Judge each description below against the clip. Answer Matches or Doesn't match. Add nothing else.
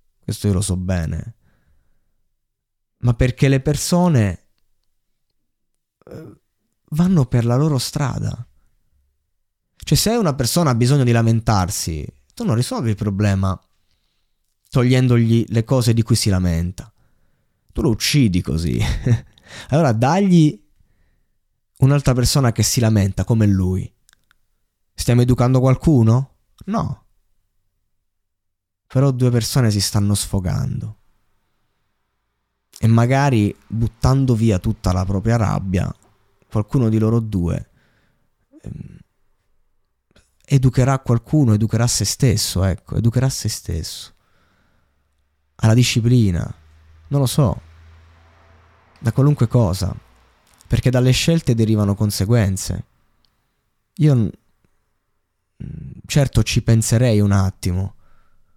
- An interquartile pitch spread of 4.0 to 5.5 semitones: Matches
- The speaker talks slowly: Matches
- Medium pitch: Doesn't match